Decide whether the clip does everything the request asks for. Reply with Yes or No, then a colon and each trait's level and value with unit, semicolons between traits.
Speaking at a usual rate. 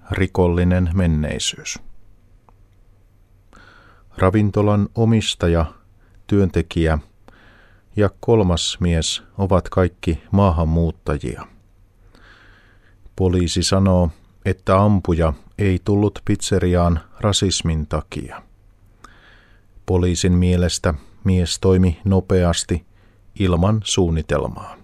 No: slow, 65 wpm